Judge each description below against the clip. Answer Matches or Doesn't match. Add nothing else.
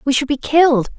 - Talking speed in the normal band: Doesn't match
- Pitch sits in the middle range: Doesn't match